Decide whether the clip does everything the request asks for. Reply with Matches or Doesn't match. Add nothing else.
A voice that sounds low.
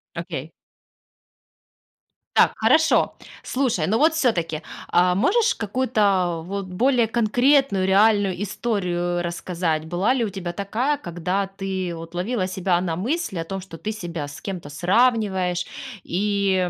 Doesn't match